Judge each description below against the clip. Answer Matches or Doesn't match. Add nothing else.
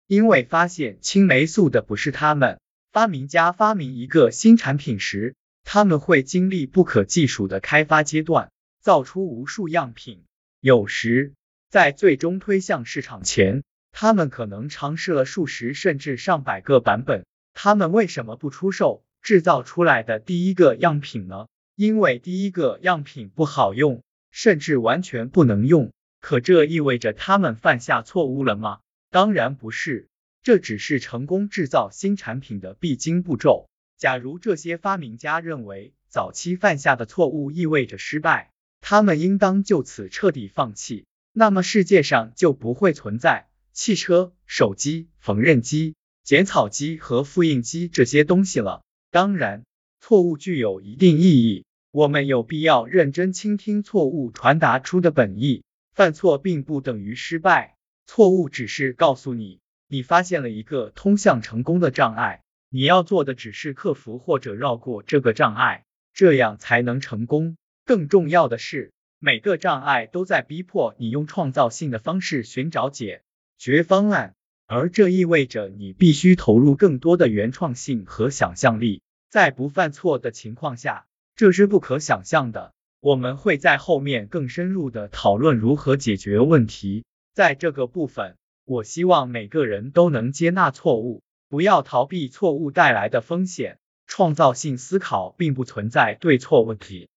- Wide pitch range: Matches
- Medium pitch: Matches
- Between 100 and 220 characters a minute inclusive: Doesn't match